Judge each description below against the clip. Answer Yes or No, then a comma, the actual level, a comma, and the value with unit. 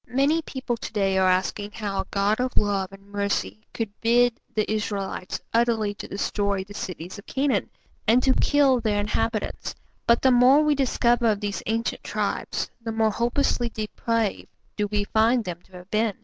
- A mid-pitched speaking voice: No, high, 215 Hz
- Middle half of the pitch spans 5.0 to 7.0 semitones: No, average, 2.9 semitones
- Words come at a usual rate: Yes, average, 180 wpm